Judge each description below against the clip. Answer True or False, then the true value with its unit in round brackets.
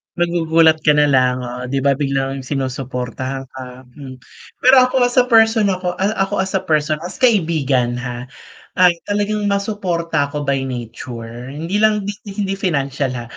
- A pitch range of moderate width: False (6.8 semitones)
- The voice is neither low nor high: True (150 Hz)